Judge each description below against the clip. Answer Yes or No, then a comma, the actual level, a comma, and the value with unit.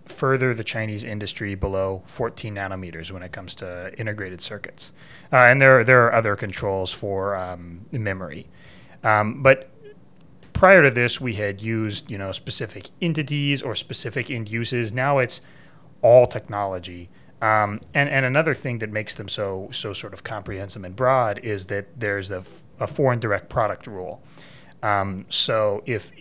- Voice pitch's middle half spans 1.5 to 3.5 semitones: No, average, 4.5 semitones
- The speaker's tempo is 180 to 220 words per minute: No, average, 165 wpm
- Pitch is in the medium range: No, low, 110 Hz